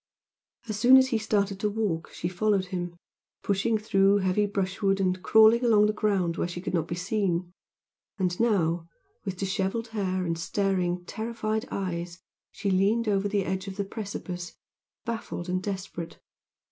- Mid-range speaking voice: No, high, 195 Hz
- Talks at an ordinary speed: Yes, average, 160 wpm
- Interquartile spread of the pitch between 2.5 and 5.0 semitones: Yes, average, 2.9 semitones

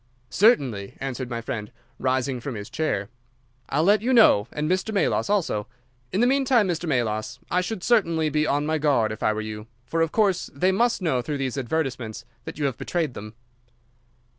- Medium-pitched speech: Yes, medium, 145 Hz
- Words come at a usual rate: Yes, average, 190 wpm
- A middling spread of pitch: No, wide, 7.5 semitones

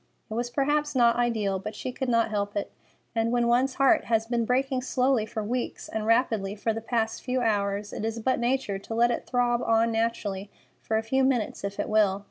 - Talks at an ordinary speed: No, fast, 220 wpm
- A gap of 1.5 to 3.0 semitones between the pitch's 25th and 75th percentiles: Yes, narrow, 2.5 semitones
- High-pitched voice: Yes, high, 230 Hz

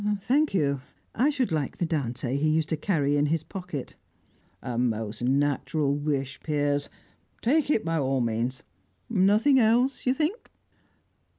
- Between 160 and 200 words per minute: No, average, 150 wpm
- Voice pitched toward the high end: No, medium, 150 Hz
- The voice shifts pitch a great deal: Yes, wide, 7.9 semitones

